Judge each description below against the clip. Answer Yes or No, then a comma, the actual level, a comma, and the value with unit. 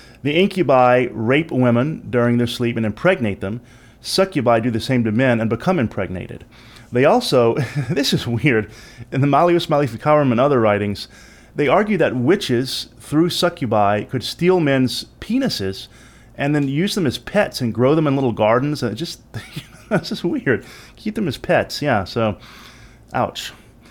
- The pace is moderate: Yes, average, 165 wpm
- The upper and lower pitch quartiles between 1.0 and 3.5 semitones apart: No, average, 4.1 semitones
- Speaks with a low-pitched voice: Yes, low, 125 Hz